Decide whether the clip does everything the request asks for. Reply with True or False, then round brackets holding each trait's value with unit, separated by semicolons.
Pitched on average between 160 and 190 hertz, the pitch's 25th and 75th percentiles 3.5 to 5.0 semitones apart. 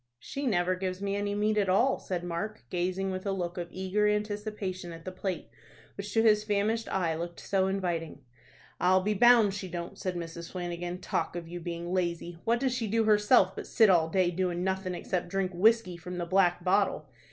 False (185 Hz; 2.9 semitones)